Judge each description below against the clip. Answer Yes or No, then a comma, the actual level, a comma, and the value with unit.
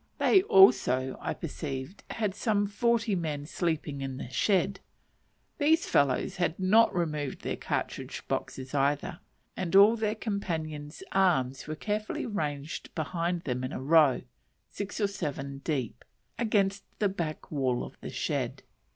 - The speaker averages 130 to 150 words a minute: Yes, average, 140 wpm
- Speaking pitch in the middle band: Yes, medium, 170 Hz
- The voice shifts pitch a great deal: Yes, wide, 6.2 semitones